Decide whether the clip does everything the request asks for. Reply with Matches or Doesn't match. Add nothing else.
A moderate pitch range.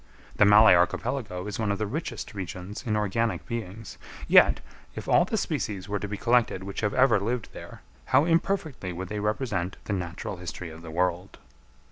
Matches